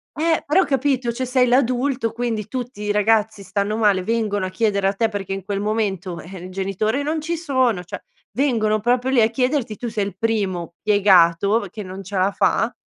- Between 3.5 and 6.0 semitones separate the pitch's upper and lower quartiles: Yes, average, 4.1 semitones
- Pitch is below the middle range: No, high, 215 Hz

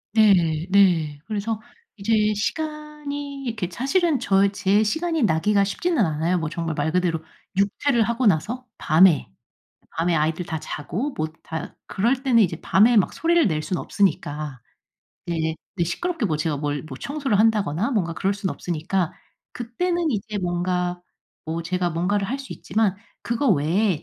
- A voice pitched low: No, high, 195 Hz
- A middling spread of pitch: No, wide, 6.2 semitones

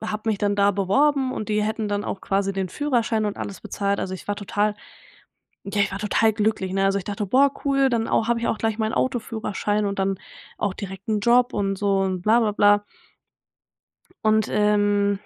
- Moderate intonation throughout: No, narrow, 1.9 semitones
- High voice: Yes, high, 210 Hz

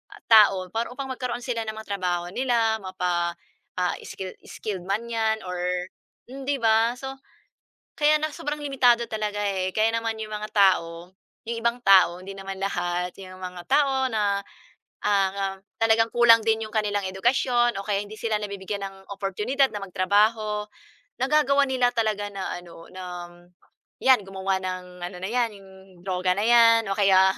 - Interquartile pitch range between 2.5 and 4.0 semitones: Yes, average, 3.5 semitones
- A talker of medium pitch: No, high, 210 Hz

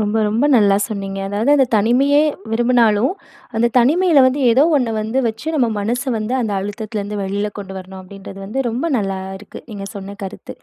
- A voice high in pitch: Yes, high, 220 Hz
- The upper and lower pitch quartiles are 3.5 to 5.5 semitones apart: Yes, average, 3.8 semitones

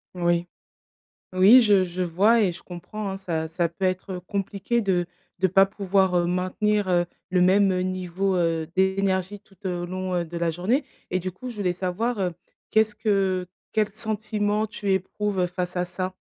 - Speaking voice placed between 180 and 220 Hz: Yes, medium, 185 Hz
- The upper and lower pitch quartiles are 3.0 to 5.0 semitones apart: No, narrow, 2.4 semitones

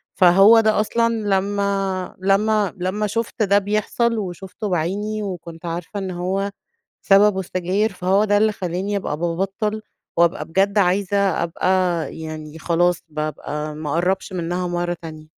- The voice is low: No, high, 190 Hz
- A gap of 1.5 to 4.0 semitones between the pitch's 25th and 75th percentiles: Yes, average, 2.9 semitones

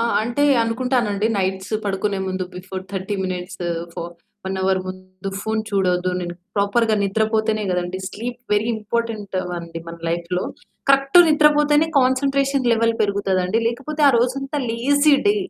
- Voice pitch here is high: Yes, high, 215 Hz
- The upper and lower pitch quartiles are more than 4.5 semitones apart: Yes, average, 5.2 semitones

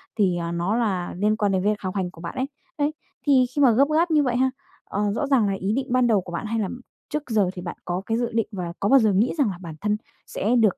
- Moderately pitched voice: No, high, 210 Hz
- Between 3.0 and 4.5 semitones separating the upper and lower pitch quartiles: No, average, 5.1 semitones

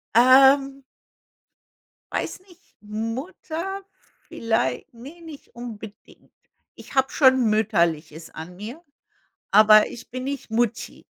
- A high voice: Yes, high, 240 Hz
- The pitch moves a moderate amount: Yes, average, 4.5 semitones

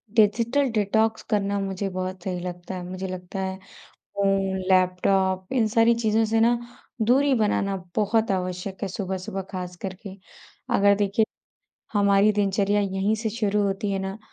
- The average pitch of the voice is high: Yes, high, 200 Hz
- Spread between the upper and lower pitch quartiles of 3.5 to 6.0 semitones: No, narrow, 2.4 semitones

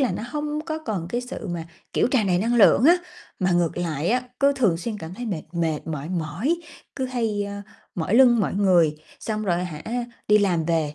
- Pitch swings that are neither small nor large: No, wide, 6.3 semitones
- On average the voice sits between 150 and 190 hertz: No, high, 200 Hz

